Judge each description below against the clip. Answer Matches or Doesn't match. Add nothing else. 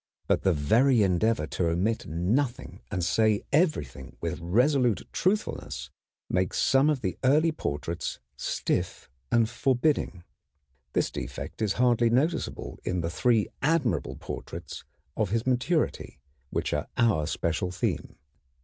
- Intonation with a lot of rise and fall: Matches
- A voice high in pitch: Doesn't match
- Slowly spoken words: Matches